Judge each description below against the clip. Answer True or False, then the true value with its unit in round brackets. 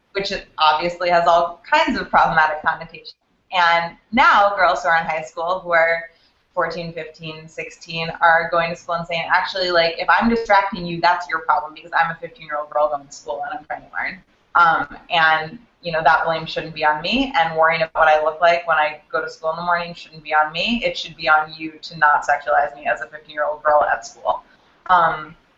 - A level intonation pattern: True (1.7 semitones)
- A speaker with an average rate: False (230 wpm)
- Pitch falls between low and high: True (165 Hz)